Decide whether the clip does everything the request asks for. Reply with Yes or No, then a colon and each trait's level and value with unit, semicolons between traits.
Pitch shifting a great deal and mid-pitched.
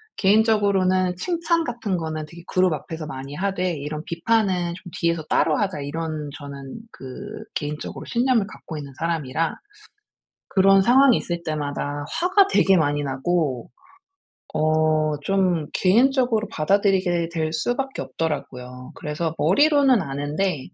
No: average, 5.0 semitones; medium, 170 Hz